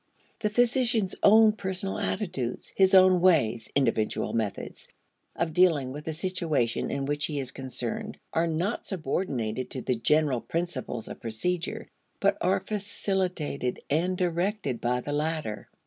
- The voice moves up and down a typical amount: No, wide, 6.4 semitones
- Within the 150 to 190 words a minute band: No, average, 140 wpm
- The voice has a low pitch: No, medium, 160 Hz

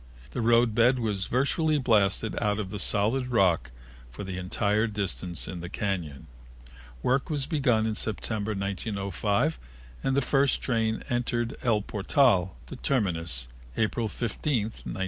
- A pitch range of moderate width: Yes, average, 3.8 semitones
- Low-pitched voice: Yes, low, 110 Hz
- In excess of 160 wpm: No, average, 140 wpm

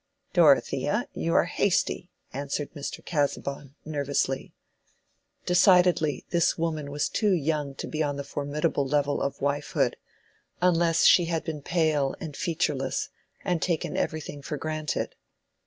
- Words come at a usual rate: No, slow, 125 wpm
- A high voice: No, medium, 150 Hz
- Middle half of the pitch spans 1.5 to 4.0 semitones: Yes, average, 2.8 semitones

